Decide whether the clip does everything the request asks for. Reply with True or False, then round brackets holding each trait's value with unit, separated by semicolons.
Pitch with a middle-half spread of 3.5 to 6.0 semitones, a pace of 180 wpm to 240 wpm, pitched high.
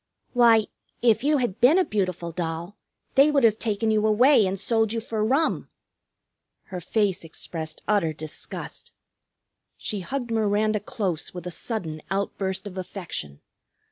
False (4.1 semitones; 145 wpm; 210 Hz)